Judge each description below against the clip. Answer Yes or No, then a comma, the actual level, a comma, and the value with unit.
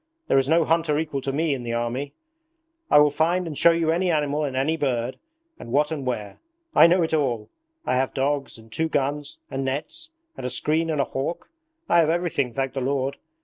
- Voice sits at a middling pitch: Yes, medium, 145 Hz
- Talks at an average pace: No, fast, 225 wpm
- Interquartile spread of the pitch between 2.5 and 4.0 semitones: Yes, average, 3.4 semitones